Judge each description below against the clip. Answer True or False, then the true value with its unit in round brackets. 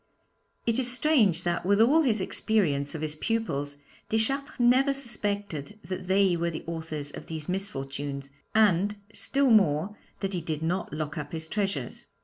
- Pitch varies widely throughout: True (5.9 semitones)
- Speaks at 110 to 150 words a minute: False (160 wpm)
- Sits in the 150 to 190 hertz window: True (185 Hz)